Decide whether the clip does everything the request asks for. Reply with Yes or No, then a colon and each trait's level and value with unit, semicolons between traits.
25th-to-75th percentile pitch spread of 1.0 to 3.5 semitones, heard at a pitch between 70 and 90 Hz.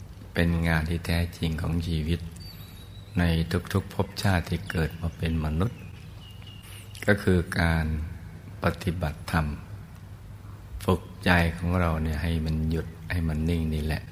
Yes: average, 2.7 semitones; very low, 85 Hz